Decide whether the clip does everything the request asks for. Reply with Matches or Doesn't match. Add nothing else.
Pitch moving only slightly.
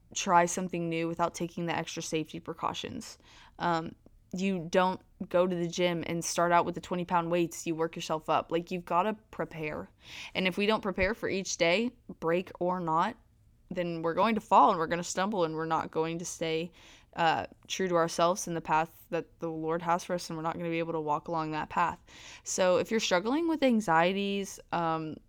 Matches